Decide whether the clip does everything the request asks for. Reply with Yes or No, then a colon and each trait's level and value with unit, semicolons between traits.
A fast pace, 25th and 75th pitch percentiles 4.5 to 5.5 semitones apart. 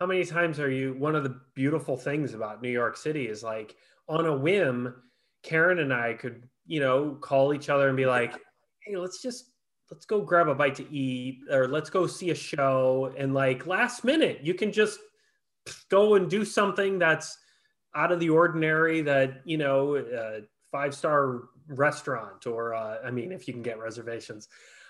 No: average, 190 wpm; average, 5.0 semitones